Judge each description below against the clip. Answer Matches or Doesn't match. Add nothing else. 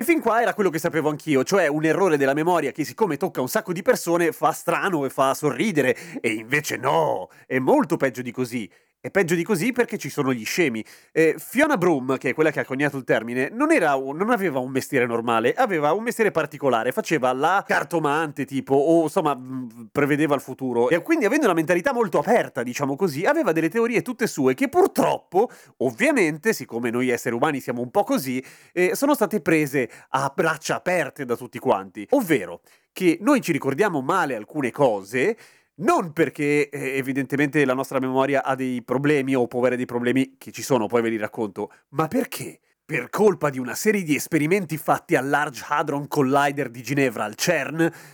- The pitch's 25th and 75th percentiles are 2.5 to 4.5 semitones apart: Doesn't match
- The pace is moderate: Doesn't match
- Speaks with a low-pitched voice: Doesn't match